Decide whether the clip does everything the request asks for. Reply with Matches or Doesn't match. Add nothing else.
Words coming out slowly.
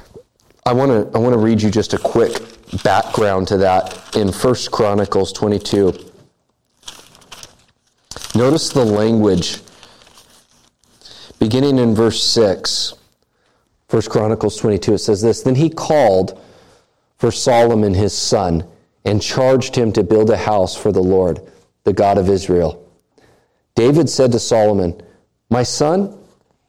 Matches